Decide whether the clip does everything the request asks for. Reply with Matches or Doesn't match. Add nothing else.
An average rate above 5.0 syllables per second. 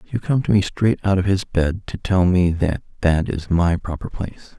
Doesn't match